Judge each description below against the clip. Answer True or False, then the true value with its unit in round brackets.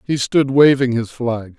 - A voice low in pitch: True (125 Hz)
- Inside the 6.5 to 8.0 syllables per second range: False (4.1 syllables/s)